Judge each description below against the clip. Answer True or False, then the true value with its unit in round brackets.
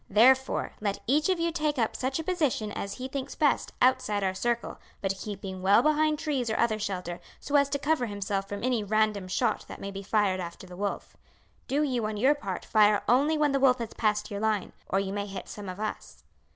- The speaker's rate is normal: False (225 wpm)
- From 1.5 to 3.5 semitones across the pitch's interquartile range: False (5.3 semitones)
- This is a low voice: False (220 Hz)